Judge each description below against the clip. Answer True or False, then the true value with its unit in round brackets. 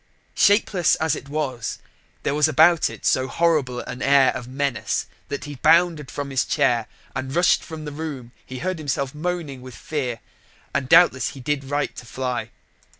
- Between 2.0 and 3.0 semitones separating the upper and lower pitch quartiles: False (3.5 semitones)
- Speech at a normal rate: True (180 wpm)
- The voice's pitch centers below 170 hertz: True (140 Hz)